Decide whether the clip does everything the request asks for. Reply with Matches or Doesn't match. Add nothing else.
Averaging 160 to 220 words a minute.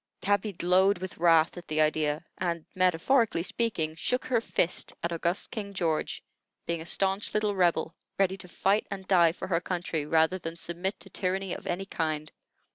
Matches